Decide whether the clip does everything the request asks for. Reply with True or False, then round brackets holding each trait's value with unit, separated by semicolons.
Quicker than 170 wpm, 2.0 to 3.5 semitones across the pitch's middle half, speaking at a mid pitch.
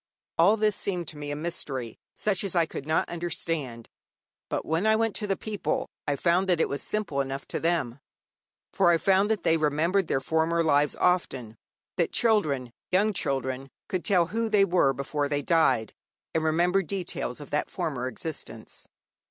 False (180 wpm; 5.0 semitones; 165 Hz)